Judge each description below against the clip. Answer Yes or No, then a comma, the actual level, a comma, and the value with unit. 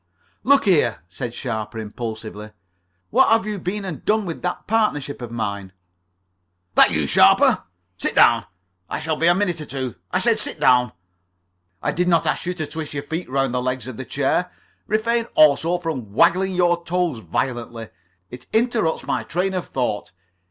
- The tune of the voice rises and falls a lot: Yes, wide, 7.0 semitones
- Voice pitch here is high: No, medium, 155 Hz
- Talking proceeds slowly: No, average, 175 wpm